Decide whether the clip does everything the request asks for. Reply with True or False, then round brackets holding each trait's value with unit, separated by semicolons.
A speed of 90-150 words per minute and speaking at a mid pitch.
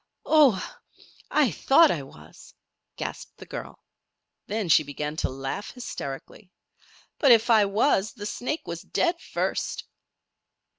False (135 wpm; 210 Hz)